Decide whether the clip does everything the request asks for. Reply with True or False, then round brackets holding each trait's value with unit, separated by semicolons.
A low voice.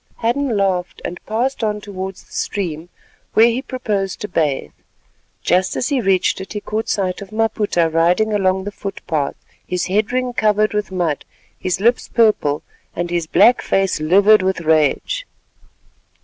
False (195 Hz)